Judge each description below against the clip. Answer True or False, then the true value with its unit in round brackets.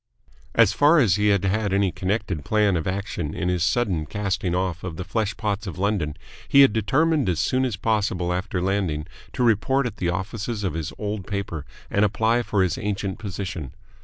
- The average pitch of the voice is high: False (100 Hz)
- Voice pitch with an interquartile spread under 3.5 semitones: True (3.1 semitones)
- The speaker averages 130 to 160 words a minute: False (195 wpm)